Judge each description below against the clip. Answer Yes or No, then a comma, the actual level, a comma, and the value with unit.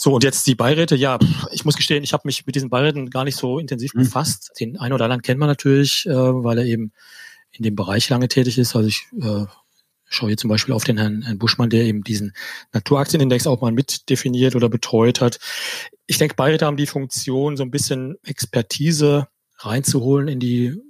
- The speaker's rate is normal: No, fast, 200 wpm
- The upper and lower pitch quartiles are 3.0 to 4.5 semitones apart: Yes, average, 3.3 semitones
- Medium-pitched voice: No, low, 130 Hz